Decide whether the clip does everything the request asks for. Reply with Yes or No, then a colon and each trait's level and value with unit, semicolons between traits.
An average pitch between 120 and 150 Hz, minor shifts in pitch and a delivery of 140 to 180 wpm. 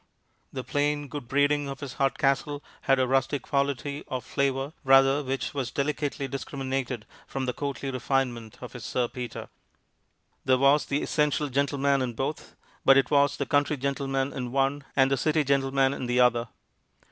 Yes: low, 135 Hz; narrow, 1.4 semitones; average, 170 wpm